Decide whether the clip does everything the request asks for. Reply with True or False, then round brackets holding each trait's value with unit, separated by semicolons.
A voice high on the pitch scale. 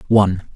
False (100 Hz)